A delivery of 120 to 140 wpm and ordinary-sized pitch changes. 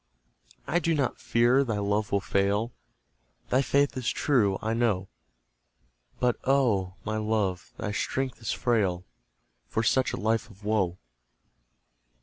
Yes: slow, 135 wpm; average, 3.8 semitones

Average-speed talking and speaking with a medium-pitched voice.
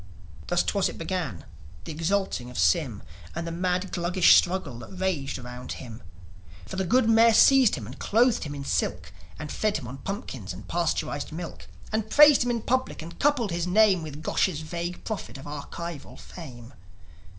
Yes: average, 180 wpm; medium, 170 Hz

